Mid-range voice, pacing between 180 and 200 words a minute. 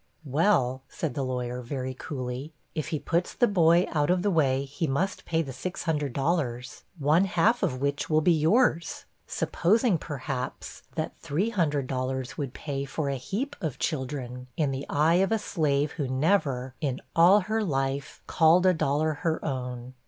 No: medium, 150 Hz; average, 165 wpm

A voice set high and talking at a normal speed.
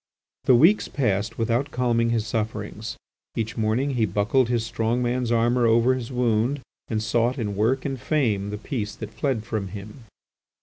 No: low, 115 Hz; average, 170 wpm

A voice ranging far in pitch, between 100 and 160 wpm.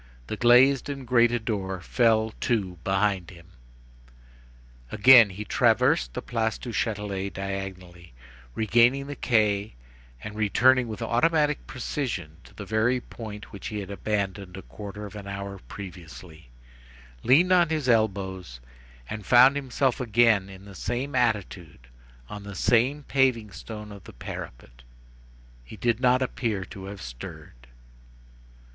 No: average, 4.1 semitones; average, 140 wpm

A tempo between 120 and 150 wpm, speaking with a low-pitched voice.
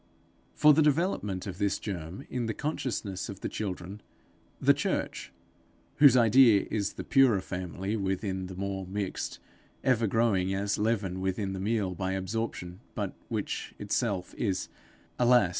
Yes: average, 145 wpm; low, 100 Hz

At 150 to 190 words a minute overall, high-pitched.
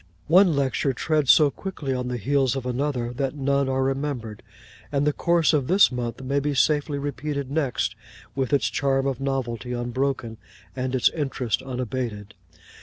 No: average, 165 wpm; low, 135 Hz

